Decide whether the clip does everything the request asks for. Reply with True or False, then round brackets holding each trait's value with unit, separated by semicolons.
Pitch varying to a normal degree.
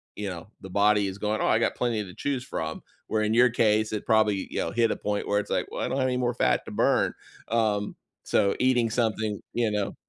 False (2.3 semitones)